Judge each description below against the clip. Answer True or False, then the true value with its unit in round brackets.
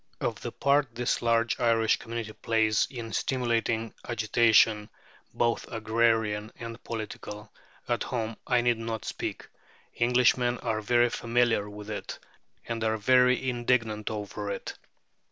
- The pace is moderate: False (130 wpm)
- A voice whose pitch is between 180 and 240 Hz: False (115 Hz)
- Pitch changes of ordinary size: False (1.7 semitones)